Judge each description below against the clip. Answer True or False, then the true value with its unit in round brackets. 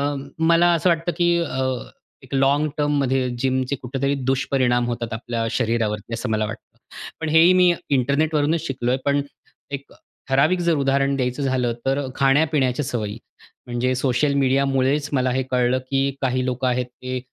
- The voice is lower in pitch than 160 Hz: True (135 Hz)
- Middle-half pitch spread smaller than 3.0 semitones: True (2.4 semitones)